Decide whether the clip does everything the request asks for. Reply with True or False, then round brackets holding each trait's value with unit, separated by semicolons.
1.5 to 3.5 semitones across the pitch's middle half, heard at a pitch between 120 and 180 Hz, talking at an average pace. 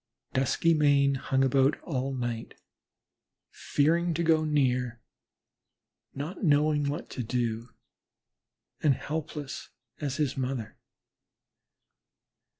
False (3.0 semitones; 140 Hz; 90 wpm)